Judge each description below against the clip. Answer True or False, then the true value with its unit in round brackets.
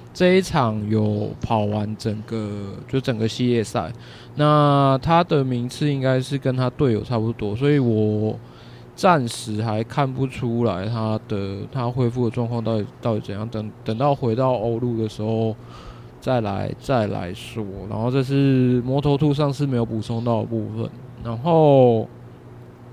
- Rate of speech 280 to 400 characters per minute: False (230 characters per minute)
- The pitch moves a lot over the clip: False (3.4 semitones)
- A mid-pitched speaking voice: False (120 Hz)